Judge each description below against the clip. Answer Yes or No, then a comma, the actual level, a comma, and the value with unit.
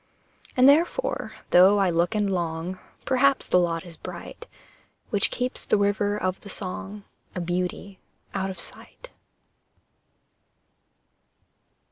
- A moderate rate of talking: No, slow, 120 wpm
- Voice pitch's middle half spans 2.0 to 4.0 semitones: Yes, average, 2.8 semitones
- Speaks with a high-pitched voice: Yes, high, 195 Hz